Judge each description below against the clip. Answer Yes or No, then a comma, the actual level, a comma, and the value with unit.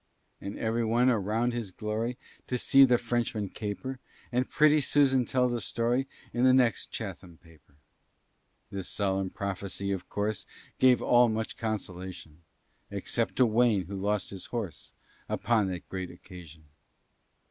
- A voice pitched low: Yes, low, 110 Hz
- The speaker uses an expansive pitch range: No, average, 4.1 semitones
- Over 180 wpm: No, average, 145 wpm